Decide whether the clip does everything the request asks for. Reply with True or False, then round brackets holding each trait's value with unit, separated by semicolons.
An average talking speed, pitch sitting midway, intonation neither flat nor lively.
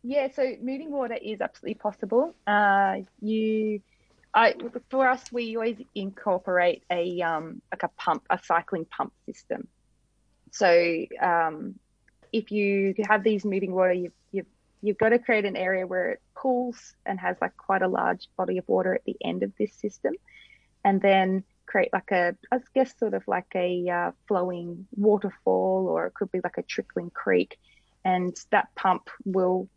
False (170 wpm; 200 Hz; 4.1 semitones)